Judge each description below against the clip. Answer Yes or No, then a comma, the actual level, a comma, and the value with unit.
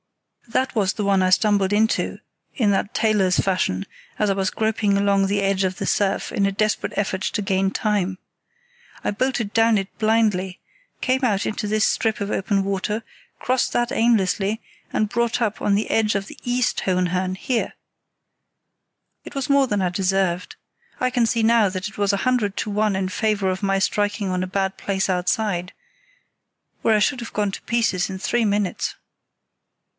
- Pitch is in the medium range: No, high, 205 Hz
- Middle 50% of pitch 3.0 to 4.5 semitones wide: No, narrow, 2.5 semitones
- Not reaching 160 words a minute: No, average, 185 wpm